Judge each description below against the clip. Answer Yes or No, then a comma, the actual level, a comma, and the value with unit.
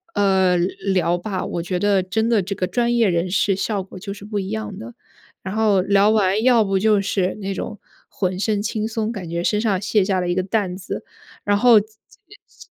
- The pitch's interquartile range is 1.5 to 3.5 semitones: Yes, narrow, 2.5 semitones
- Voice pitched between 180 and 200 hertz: Yes, high, 195 Hz